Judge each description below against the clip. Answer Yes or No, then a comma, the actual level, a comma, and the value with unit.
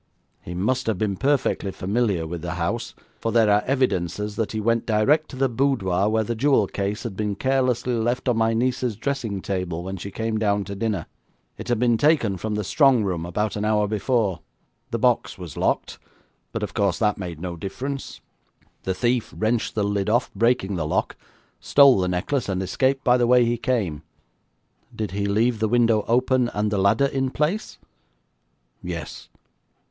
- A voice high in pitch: No, low, 110 Hz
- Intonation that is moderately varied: Yes, average, 3.9 semitones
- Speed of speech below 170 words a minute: No, average, 185 wpm